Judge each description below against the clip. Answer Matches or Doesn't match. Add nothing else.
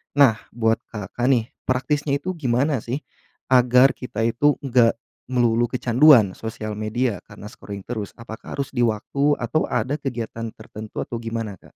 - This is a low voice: Matches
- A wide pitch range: Doesn't match